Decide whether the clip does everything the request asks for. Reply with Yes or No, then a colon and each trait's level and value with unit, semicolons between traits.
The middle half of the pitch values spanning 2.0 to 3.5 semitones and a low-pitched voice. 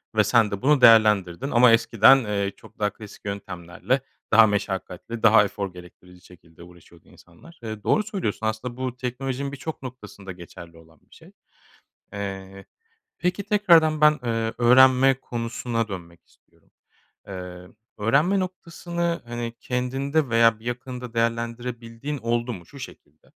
No: average, 4.7 semitones; low, 115 Hz